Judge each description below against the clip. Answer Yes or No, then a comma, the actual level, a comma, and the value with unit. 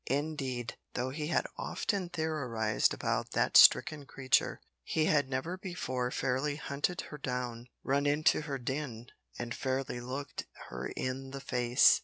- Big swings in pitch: No, average, 3.2 semitones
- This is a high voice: No, low, 135 Hz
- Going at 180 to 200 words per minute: No, average, 150 wpm